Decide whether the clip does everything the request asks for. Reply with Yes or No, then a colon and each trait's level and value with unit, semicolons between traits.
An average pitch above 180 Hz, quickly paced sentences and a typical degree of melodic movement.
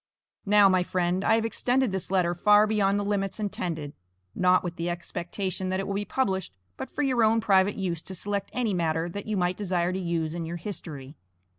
Yes: high, 190 Hz; fast, 210 wpm; average, 3.0 semitones